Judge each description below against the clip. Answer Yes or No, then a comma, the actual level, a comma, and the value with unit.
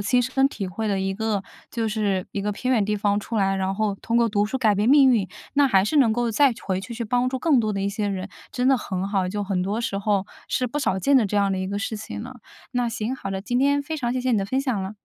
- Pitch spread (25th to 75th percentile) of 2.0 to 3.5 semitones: No, average, 4.0 semitones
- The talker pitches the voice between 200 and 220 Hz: Yes, high, 215 Hz